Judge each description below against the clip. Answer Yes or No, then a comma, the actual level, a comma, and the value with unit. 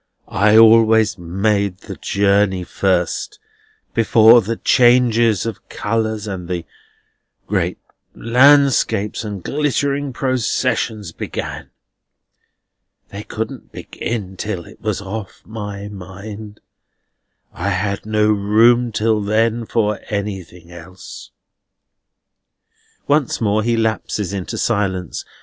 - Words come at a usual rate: No, slow, 100 wpm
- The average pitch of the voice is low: Yes, low, 105 Hz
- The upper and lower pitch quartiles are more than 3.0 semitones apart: No, narrow, 2.6 semitones